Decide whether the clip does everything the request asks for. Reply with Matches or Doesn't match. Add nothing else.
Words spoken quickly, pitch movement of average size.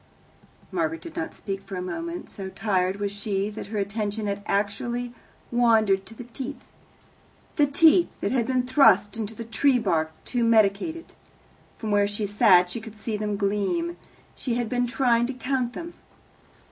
Doesn't match